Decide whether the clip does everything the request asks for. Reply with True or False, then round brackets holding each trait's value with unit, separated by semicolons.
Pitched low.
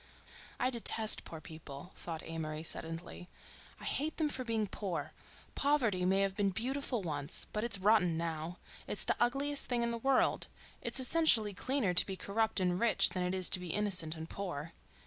False (195 Hz)